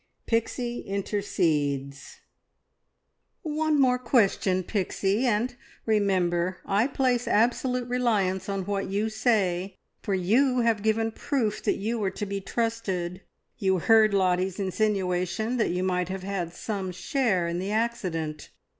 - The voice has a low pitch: No, high, 200 Hz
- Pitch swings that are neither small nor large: Yes, average, 3.8 semitones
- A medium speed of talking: No, slow, 130 wpm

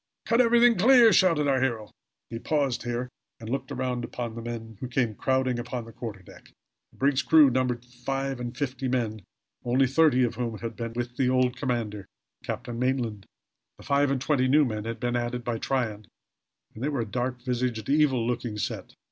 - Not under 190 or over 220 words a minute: Yes, average, 200 wpm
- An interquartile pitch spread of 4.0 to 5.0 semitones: No, narrow, 2.4 semitones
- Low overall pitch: Yes, low, 125 Hz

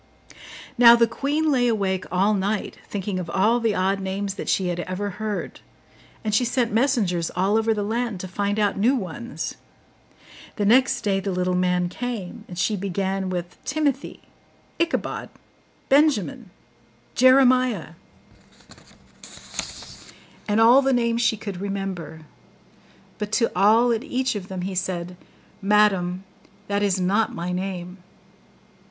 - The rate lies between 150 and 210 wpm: No, average, 140 wpm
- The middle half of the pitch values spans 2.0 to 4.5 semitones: Yes, average, 4.0 semitones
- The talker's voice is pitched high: Yes, high, 205 Hz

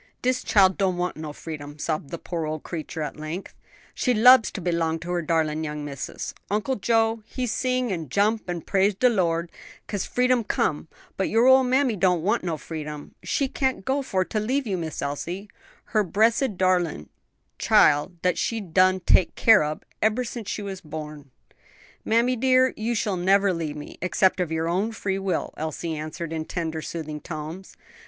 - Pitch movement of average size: No, wide, 5.7 semitones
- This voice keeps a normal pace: Yes, average, 185 wpm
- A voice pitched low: No, medium, 185 Hz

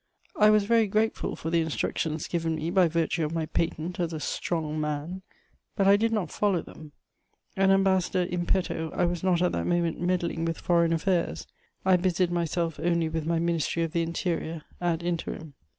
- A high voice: No, medium, 170 Hz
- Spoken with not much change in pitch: Yes, narrow, 2.0 semitones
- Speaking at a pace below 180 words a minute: No, average, 190 wpm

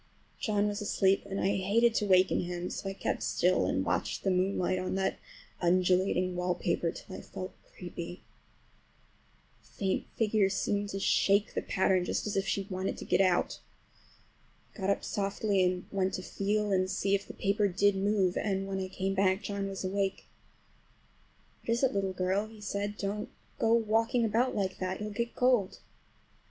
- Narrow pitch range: Yes, narrow, 1.8 semitones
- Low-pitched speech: No, high, 195 Hz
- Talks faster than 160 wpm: Yes, average, 180 wpm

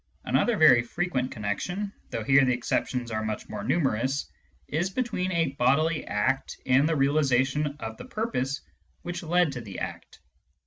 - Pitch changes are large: Yes, wide, 5.7 semitones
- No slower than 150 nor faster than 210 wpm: Yes, average, 160 wpm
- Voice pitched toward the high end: No, medium, 140 Hz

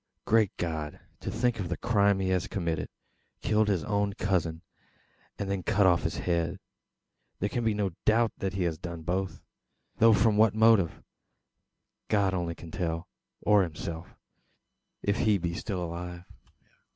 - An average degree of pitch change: Yes, average, 3.4 semitones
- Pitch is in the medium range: No, very low, 95 Hz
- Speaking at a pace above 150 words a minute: Yes, average, 160 wpm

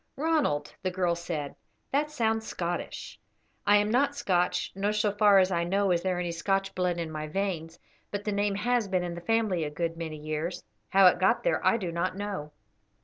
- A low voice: No, medium, 185 Hz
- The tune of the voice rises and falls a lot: No, average, 3.4 semitones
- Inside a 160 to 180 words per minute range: No, fast, 205 wpm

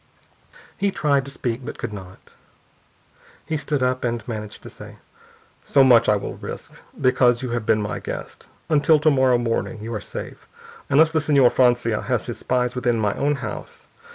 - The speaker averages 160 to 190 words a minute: Yes, average, 180 wpm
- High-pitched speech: No, low, 125 Hz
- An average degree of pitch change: Yes, average, 3.4 semitones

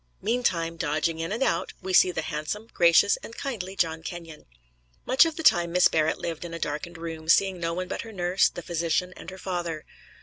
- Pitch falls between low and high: Yes, medium, 170 Hz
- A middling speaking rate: No, fast, 210 wpm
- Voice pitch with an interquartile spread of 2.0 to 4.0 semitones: Yes, narrow, 2.4 semitones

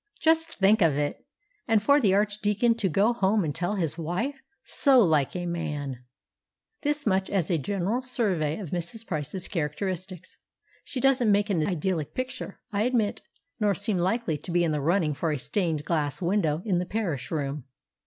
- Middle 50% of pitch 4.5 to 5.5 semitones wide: Yes, average, 5.2 semitones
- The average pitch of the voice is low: No, medium, 185 Hz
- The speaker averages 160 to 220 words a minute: Yes, average, 180 wpm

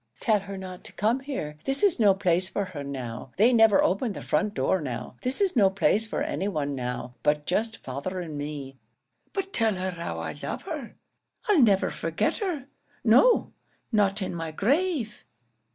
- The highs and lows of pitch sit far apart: Yes, wide, 7.1 semitones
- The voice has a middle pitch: No, high, 195 Hz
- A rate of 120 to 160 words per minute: No, average, 185 wpm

